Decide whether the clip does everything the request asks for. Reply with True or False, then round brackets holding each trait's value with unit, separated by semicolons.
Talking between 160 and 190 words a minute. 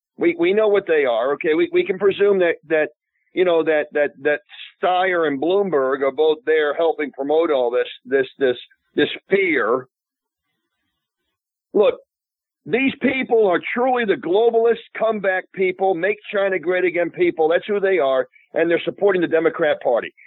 True (165 wpm)